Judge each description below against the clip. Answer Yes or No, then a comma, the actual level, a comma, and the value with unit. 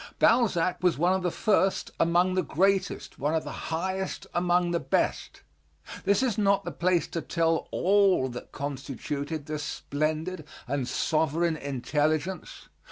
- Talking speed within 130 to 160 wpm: Yes, average, 145 wpm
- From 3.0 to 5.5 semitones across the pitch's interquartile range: Yes, average, 3.6 semitones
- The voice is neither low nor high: Yes, medium, 170 Hz